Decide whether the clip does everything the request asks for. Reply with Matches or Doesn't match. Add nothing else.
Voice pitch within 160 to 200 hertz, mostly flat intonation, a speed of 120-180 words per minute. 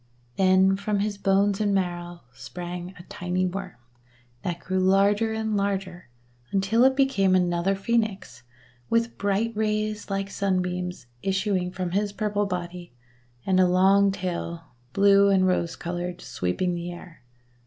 Matches